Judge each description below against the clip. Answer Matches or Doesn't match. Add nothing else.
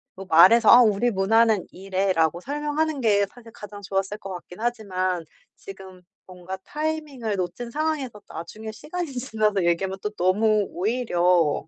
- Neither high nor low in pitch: Doesn't match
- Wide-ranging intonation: Doesn't match